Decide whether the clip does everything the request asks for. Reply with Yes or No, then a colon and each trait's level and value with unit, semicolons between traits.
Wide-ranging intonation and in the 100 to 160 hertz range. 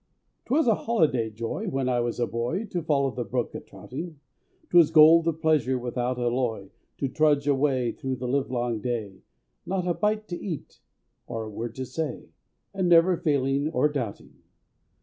No: average, 5.0 semitones; low, 135 Hz